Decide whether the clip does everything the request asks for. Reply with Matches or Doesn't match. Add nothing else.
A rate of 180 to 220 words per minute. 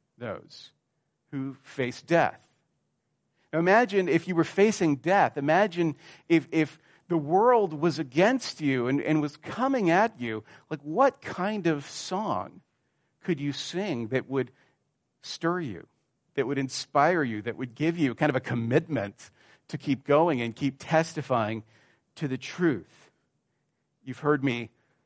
Doesn't match